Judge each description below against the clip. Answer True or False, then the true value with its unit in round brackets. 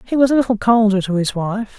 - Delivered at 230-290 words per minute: True (270 wpm)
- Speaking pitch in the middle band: False (215 Hz)